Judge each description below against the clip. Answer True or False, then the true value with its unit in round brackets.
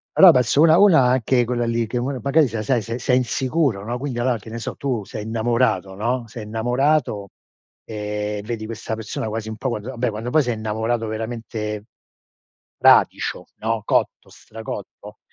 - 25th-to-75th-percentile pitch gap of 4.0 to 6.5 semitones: False (2.6 semitones)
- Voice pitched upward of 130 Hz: False (115 Hz)